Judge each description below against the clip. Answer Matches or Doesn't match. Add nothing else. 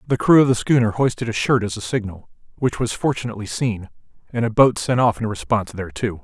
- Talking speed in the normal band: Doesn't match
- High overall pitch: Doesn't match